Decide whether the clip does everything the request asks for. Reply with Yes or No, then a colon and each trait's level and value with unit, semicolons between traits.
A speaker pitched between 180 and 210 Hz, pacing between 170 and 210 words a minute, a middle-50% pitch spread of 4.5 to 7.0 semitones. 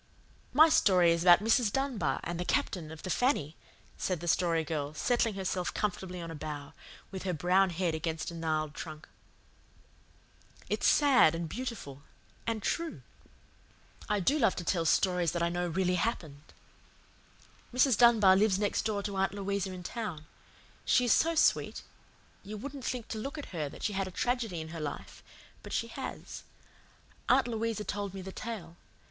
Yes: medium, 185 Hz; average, 175 wpm; average, 4.9 semitones